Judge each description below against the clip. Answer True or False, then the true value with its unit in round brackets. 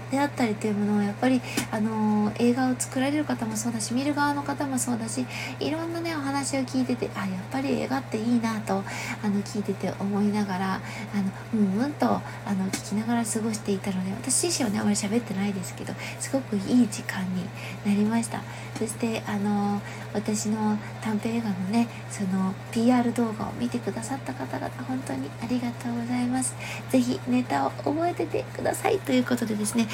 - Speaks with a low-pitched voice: False (200 Hz)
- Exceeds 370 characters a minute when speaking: True (385 characters per minute)